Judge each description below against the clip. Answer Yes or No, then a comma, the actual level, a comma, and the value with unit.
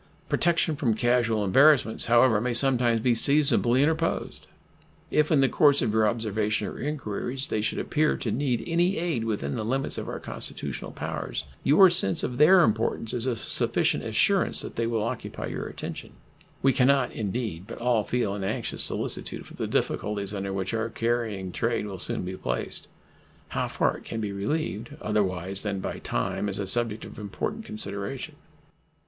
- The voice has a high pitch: No, low, 115 Hz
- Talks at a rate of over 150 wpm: Yes, average, 175 wpm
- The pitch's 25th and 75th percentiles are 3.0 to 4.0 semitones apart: No, average, 4.5 semitones